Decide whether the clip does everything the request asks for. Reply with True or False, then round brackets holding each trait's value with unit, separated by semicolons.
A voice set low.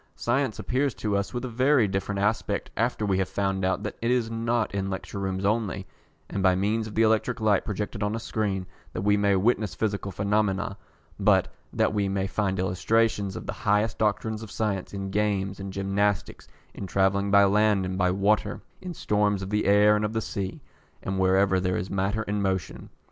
True (100 Hz)